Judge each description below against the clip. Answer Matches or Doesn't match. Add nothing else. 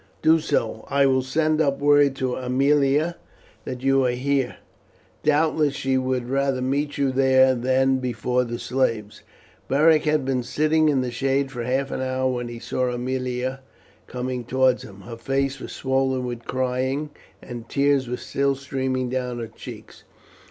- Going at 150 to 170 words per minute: Matches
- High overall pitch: Doesn't match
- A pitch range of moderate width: Doesn't match